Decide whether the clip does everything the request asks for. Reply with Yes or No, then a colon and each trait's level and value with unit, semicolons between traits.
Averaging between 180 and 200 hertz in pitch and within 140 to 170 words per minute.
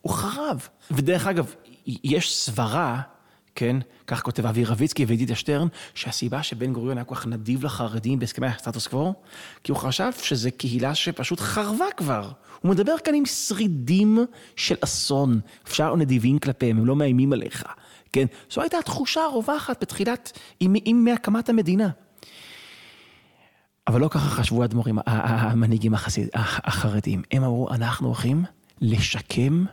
No: low, 135 Hz; average, 145 wpm